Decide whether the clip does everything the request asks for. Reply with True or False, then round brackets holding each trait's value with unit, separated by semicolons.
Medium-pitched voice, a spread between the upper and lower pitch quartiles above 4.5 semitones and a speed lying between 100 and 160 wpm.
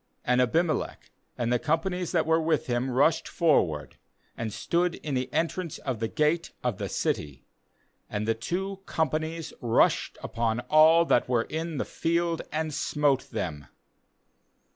True (150 Hz; 5.6 semitones; 155 wpm)